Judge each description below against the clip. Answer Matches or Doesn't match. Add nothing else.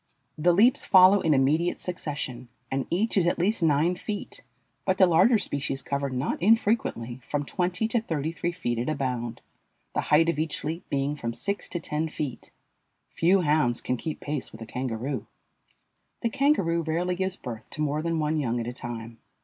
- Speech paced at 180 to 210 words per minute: Matches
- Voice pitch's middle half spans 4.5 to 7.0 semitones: Matches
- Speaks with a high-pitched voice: Doesn't match